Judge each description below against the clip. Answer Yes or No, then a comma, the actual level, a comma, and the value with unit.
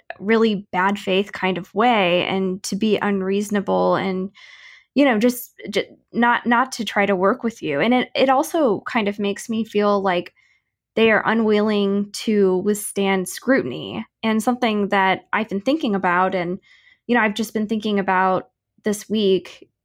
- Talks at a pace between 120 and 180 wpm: Yes, average, 170 wpm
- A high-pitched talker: Yes, high, 205 Hz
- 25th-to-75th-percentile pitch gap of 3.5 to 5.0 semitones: No, average, 2.9 semitones